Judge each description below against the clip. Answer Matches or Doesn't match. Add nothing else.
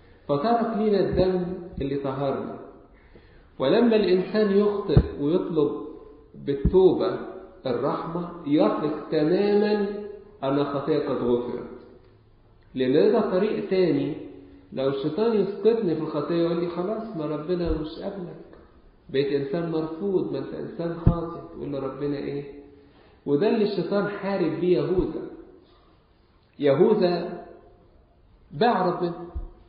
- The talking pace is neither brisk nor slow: Matches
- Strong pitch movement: Matches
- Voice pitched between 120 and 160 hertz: Doesn't match